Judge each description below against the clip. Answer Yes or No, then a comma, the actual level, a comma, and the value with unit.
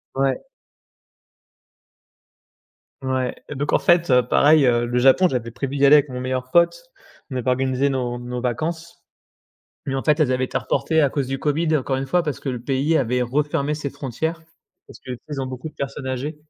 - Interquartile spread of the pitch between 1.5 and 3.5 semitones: Yes, average, 2.8 semitones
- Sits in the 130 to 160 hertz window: Yes, low, 135 Hz